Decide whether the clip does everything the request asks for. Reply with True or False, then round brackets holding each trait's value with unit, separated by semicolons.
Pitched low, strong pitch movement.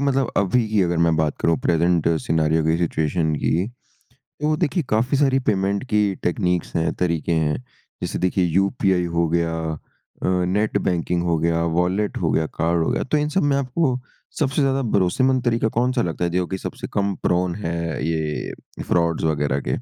True (90 Hz; 5.9 semitones)